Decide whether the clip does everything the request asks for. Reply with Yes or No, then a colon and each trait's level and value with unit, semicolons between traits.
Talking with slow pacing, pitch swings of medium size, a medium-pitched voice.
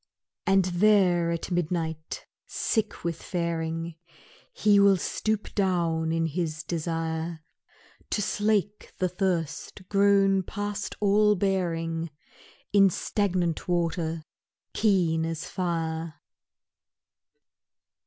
Yes: slow, 95 wpm; average, 3.2 semitones; medium, 175 Hz